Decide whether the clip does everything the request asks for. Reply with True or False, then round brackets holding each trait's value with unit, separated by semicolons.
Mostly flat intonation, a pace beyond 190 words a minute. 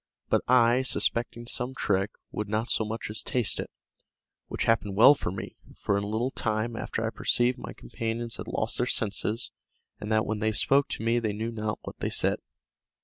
True (1.8 semitones; 200 wpm)